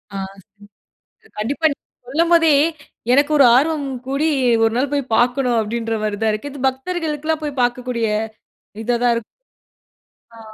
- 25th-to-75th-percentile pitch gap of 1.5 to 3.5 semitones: No, average, 4.1 semitones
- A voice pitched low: No, very high, 265 Hz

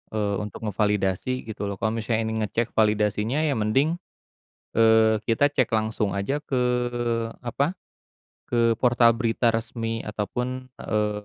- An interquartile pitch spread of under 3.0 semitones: Yes, narrow, 2.5 semitones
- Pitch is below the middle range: Yes, low, 115 Hz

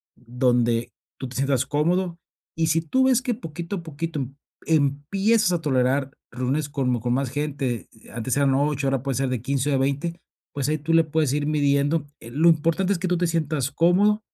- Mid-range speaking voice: Yes, medium, 145 Hz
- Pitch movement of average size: Yes, average, 3.7 semitones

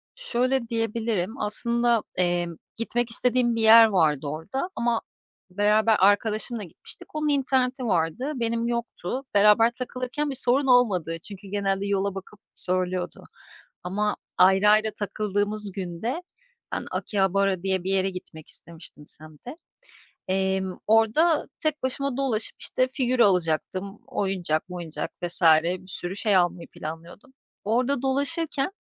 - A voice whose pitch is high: Yes, high, 210 Hz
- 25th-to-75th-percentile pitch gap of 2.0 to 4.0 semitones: No, average, 4.8 semitones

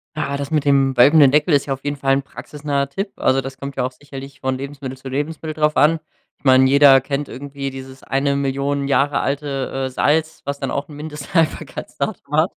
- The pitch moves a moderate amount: No, narrow, 1.4 semitones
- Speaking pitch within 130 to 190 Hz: Yes, medium, 140 Hz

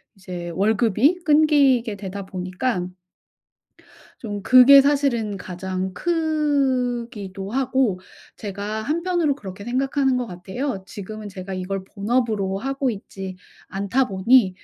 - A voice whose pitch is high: Yes, high, 220 Hz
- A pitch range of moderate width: No, wide, 5.8 semitones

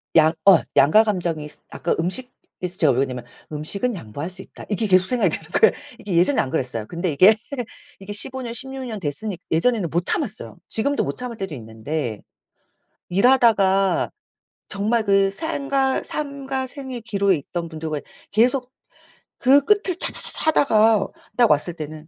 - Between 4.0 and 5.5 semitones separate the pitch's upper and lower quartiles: No, wide, 7.6 semitones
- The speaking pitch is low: No, high, 195 Hz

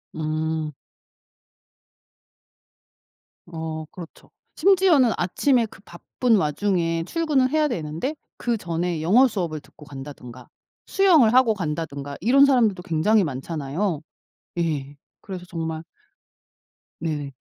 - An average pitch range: No, wide, 7.2 semitones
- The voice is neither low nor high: Yes, medium, 170 Hz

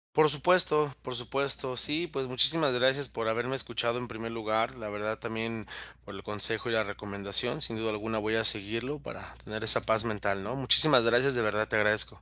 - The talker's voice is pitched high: No, low, 115 Hz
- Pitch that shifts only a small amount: No, average, 3.3 semitones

